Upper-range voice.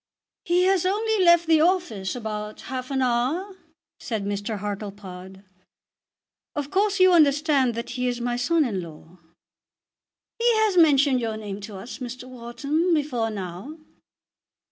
Yes: very high, 255 Hz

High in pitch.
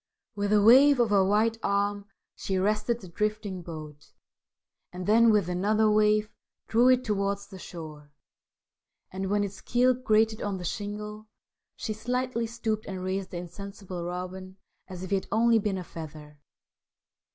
Yes: high, 205 Hz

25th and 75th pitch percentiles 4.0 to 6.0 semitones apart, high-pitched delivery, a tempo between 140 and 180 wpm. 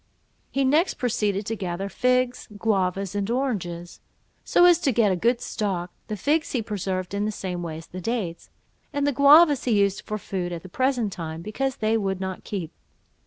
No: average, 5.3 semitones; high, 210 Hz; average, 195 wpm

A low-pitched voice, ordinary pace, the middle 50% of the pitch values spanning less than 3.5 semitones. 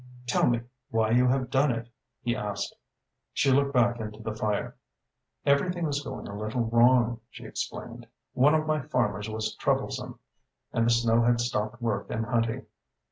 Yes: low, 120 Hz; average, 170 wpm; average, 2.9 semitones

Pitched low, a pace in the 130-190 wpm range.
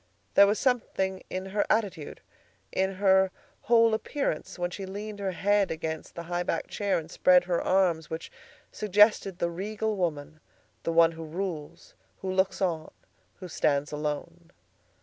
No: medium, 185 Hz; average, 155 wpm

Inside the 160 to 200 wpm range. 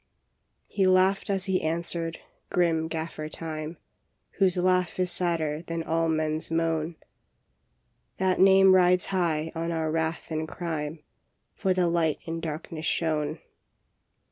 No: average, 145 wpm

